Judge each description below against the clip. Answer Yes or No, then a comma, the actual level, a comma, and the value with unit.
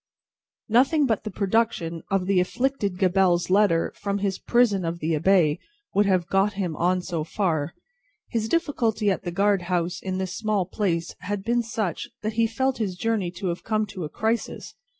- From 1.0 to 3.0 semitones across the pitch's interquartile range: No, average, 3.6 semitones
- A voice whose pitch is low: No, high, 195 Hz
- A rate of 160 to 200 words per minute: Yes, average, 185 wpm